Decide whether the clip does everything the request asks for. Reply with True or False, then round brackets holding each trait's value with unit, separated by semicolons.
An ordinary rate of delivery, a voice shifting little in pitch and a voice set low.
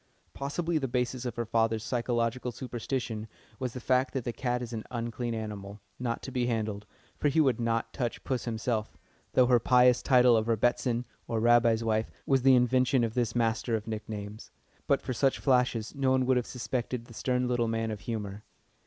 True (195 wpm; 2.1 semitones; 120 Hz)